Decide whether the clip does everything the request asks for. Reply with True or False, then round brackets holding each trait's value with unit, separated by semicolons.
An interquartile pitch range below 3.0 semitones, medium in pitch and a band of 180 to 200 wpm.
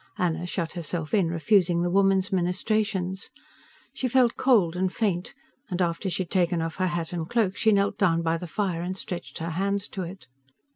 True (2.6 semitones; 180 Hz; 195 wpm)